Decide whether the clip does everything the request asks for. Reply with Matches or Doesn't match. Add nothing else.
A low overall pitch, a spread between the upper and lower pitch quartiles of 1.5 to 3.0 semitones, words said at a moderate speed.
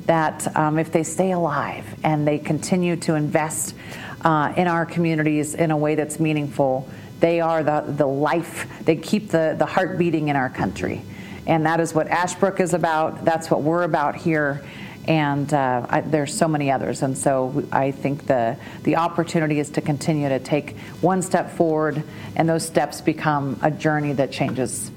Doesn't match